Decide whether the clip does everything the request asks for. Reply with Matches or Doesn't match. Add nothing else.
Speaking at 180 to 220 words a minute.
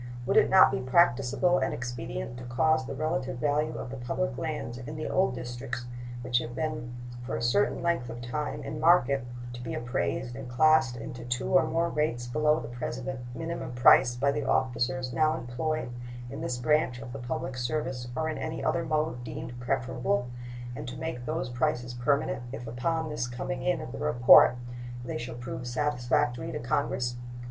Matches